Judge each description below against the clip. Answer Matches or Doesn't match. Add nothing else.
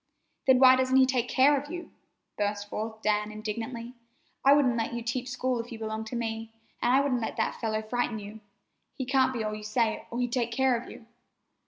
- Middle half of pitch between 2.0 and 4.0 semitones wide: Matches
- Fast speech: Matches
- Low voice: Doesn't match